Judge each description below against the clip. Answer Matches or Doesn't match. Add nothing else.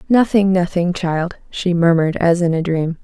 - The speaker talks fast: Doesn't match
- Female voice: Matches